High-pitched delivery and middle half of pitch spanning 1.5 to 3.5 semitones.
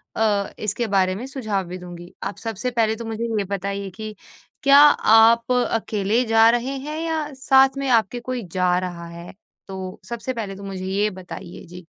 No: high, 215 Hz; average, 4.2 semitones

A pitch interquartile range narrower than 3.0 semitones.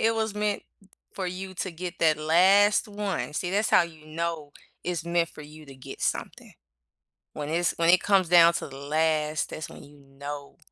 No: average, 3.5 semitones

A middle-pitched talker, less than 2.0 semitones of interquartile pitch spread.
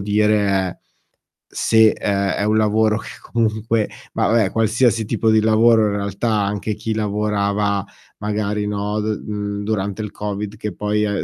No: low, 105 Hz; narrow, 1.2 semitones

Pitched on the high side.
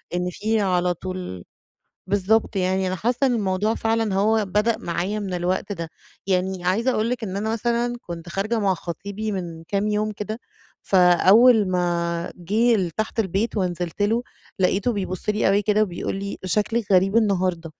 Yes: high, 195 Hz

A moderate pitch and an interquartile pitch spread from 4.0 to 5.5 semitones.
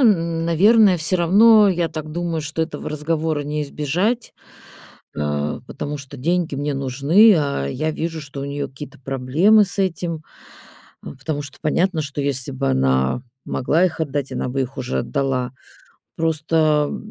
No: medium, 150 Hz; average, 3.6 semitones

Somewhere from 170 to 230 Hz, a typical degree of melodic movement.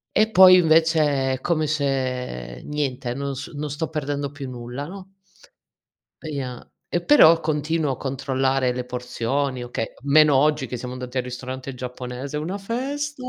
No: medium, 140 Hz; average, 3.6 semitones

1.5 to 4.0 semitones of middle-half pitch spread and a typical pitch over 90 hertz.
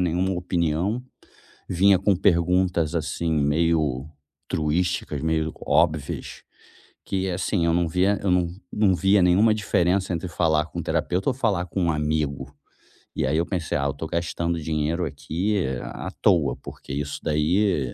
No: average, 3.2 semitones; very low, 85 Hz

